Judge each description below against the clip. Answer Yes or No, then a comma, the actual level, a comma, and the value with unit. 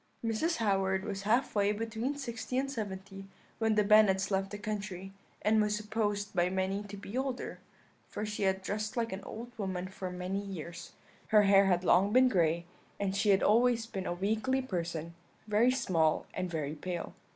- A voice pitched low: No, high, 205 Hz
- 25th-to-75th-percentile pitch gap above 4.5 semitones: No, narrow, 2.6 semitones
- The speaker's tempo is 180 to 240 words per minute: Yes, average, 185 wpm